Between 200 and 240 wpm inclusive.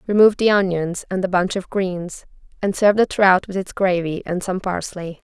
Yes: fast, 205 wpm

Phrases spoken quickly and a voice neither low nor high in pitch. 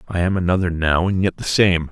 No: fast, 250 wpm; very low, 90 Hz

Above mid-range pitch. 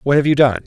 No: low, 130 Hz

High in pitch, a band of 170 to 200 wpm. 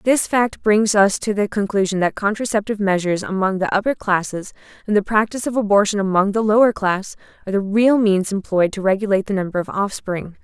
Yes: high, 200 Hz; average, 195 wpm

